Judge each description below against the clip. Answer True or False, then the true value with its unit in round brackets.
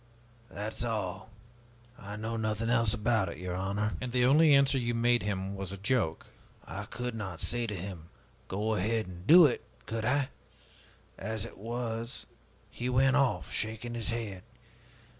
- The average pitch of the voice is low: True (110 Hz)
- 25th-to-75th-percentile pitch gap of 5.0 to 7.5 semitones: False (3.2 semitones)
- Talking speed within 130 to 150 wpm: False (170 wpm)